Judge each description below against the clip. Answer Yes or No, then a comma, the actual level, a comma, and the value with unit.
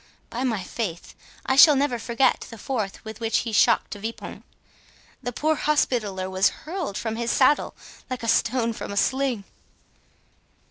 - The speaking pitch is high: Yes, high, 230 Hz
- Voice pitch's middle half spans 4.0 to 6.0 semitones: No, average, 3.5 semitones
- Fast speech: No, average, 165 wpm